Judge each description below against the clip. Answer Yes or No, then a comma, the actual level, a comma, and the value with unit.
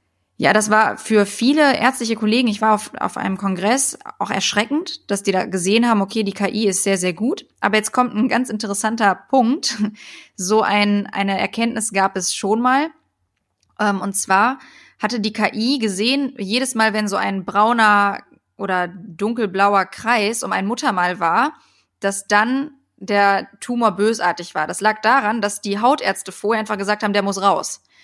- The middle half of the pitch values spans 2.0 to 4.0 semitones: Yes, average, 2.8 semitones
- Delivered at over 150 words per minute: Yes, average, 170 wpm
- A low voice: No, high, 210 Hz